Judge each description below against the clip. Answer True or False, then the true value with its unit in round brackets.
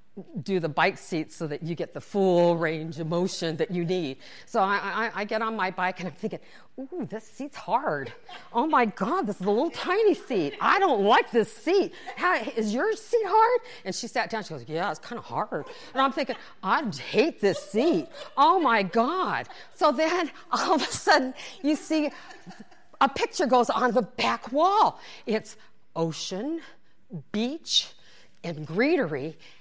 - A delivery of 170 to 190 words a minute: True (185 wpm)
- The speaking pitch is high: True (225 Hz)